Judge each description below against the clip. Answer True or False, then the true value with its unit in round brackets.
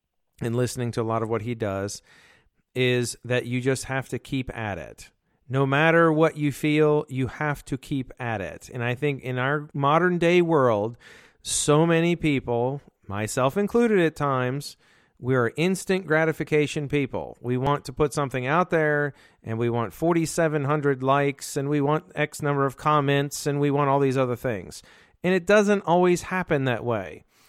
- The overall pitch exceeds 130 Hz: True (140 Hz)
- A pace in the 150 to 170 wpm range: False (180 wpm)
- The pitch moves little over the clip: False (3.8 semitones)